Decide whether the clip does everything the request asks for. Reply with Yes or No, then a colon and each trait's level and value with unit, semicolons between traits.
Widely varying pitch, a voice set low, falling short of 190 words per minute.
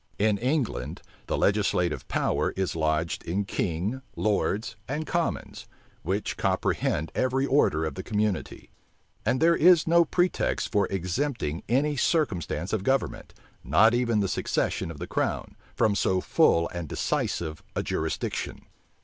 Yes: wide, 7.2 semitones; low, 105 Hz; average, 140 wpm